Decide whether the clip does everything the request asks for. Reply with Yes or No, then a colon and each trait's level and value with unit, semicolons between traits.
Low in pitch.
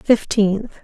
No: high, 210 Hz